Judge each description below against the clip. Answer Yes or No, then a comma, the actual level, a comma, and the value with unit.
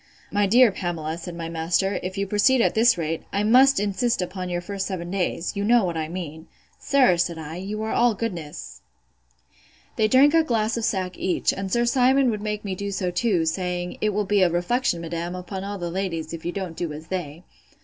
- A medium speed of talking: No, fast, 220 wpm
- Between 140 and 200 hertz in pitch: Yes, high, 190 Hz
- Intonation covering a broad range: No, average, 3.7 semitones